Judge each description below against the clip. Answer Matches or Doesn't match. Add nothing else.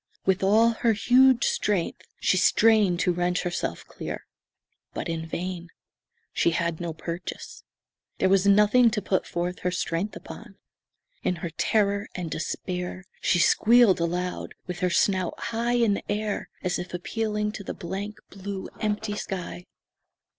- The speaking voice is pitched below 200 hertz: Matches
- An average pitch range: Matches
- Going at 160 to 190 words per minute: Doesn't match